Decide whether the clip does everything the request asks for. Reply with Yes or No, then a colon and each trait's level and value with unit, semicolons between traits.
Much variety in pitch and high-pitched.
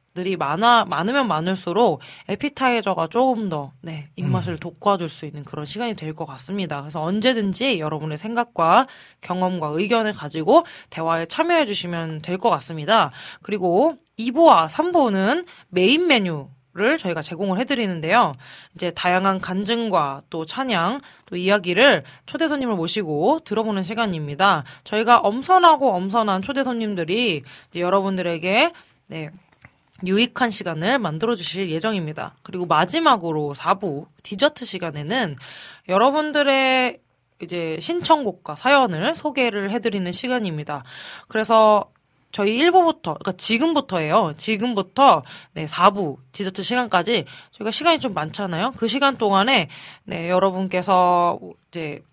Yes: wide, 6.4 semitones; high, 195 Hz